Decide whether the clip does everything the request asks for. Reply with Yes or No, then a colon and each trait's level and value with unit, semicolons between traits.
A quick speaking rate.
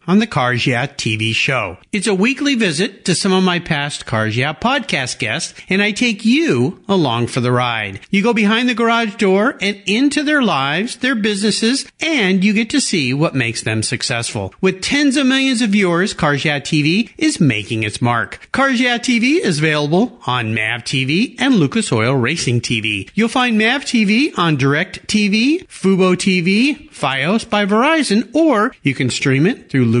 No: average, 185 wpm